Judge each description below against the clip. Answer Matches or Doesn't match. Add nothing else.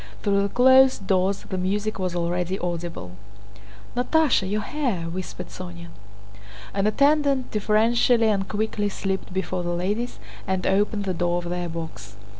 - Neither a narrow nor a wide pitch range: Matches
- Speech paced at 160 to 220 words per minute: Doesn't match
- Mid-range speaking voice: Doesn't match